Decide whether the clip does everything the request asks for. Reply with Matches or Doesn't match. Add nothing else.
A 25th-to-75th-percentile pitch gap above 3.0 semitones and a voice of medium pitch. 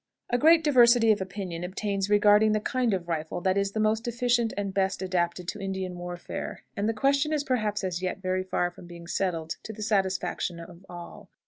Doesn't match